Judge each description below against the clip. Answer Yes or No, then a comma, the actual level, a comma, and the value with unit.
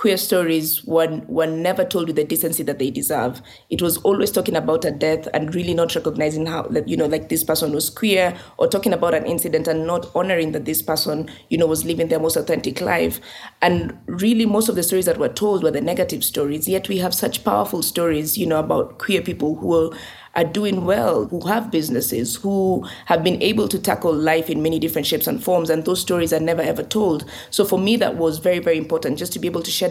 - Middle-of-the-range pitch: Yes, medium, 165 Hz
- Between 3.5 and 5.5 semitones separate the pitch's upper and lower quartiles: No, average, 2.7 semitones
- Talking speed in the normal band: No, fast, 235 wpm